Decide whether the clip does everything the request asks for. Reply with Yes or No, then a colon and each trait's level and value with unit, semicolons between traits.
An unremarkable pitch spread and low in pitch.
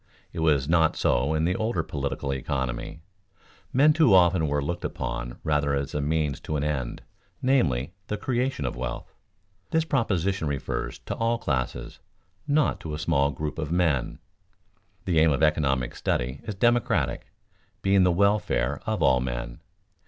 No: wide, 5.8 semitones; very low, 75 Hz